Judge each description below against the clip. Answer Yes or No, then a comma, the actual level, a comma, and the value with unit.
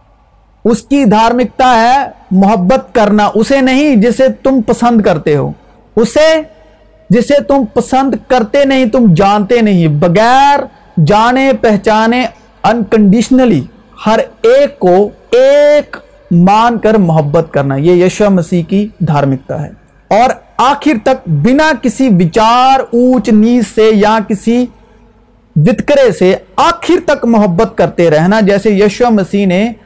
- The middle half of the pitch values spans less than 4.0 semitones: No, average, 4.6 semitones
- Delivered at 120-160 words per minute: Yes, average, 125 wpm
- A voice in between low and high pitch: No, high, 225 Hz